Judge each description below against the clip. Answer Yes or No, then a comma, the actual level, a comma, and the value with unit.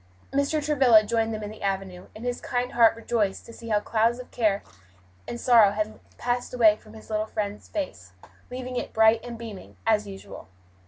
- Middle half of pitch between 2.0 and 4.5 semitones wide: Yes, narrow, 2.5 semitones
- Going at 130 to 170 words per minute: No, fast, 205 wpm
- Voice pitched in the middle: No, high, 225 Hz